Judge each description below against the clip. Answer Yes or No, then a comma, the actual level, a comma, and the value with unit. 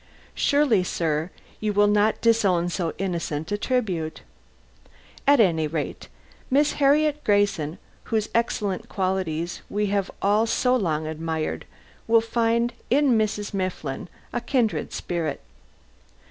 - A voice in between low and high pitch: No, high, 205 Hz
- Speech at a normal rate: No, slow, 120 wpm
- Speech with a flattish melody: No, wide, 5.4 semitones